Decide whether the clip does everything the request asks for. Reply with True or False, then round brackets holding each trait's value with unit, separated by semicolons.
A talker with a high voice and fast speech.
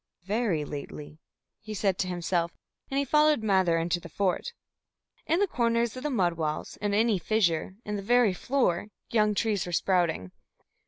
False (200 Hz; 170 wpm)